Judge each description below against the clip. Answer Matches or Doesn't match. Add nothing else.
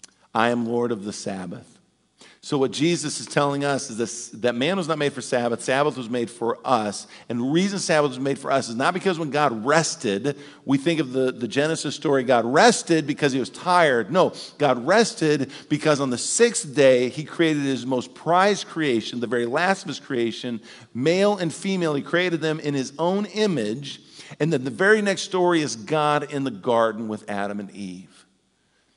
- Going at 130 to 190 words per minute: Doesn't match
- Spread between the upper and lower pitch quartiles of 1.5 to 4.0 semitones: Doesn't match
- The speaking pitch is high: Doesn't match